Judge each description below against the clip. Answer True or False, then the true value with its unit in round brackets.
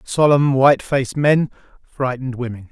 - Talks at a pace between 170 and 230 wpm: False (135 wpm)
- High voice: False (135 Hz)